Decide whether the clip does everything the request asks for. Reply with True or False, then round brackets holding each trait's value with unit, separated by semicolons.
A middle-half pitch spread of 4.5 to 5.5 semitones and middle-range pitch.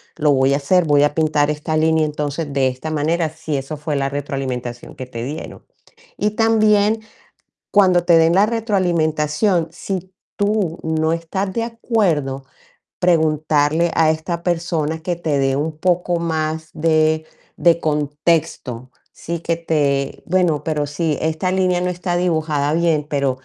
False (3.0 semitones; 160 Hz)